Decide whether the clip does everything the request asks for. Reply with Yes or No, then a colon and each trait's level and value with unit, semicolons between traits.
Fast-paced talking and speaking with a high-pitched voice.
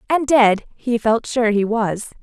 No: average, 190 wpm; high, 230 Hz